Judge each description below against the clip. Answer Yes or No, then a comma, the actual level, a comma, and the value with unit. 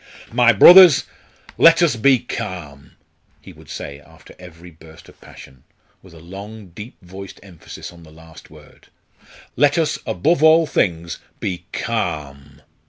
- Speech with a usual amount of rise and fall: No, wide, 7.2 semitones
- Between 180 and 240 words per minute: No, average, 145 wpm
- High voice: No, very low, 90 Hz